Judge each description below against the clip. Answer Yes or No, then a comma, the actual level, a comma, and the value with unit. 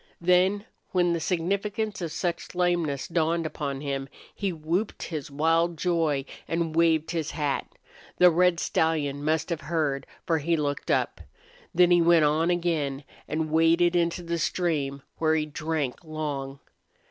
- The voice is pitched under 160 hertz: No, medium, 165 Hz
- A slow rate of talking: No, average, 150 wpm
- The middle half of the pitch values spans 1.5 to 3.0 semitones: Yes, narrow, 2.4 semitones